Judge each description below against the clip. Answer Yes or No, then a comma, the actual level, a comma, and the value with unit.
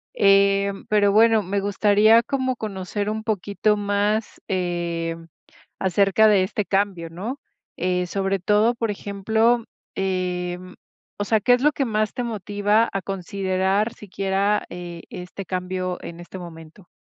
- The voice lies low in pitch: No, high, 200 Hz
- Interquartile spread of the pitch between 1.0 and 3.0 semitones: Yes, average, 2.7 semitones